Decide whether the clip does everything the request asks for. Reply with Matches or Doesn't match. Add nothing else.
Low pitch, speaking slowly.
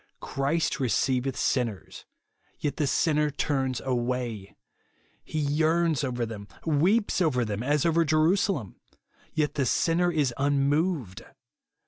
Doesn't match